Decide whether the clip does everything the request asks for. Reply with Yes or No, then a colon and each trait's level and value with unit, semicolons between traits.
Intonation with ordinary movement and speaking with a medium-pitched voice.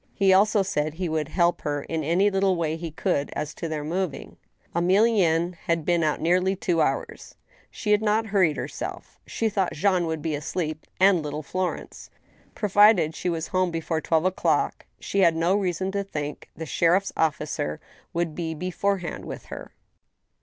Yes: average, 3.2 semitones; medium, 175 Hz